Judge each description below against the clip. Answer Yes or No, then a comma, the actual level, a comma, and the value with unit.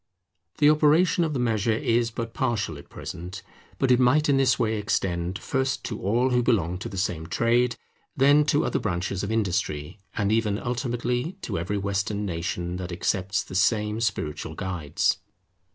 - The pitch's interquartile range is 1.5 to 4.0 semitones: No, average, 4.8 semitones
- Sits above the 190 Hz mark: No, low, 110 Hz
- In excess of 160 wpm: Yes, average, 170 wpm